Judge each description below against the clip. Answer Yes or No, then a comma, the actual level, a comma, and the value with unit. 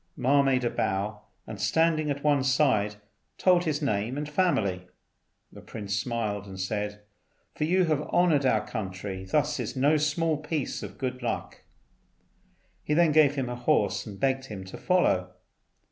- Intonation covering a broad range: Yes, wide, 6.5 semitones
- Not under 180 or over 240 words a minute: No, average, 170 wpm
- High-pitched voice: No, low, 130 Hz